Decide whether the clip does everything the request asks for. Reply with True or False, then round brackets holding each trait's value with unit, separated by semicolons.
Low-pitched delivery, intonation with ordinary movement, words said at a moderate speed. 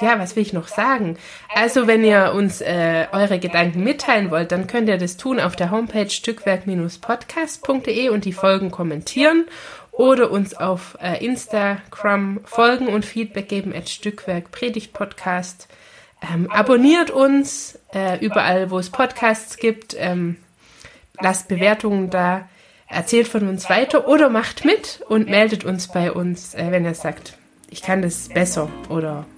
False (200 Hz; 4.2 semitones; 150 wpm)